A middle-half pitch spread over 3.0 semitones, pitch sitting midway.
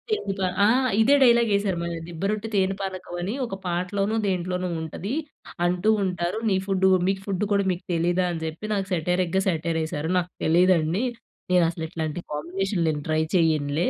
No: average, 2.7 semitones; medium, 180 Hz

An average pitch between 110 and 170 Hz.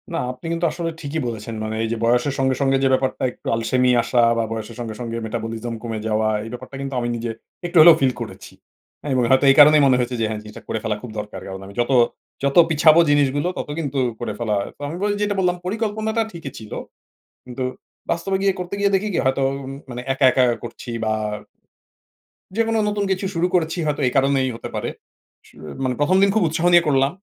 Yes: low, 135 Hz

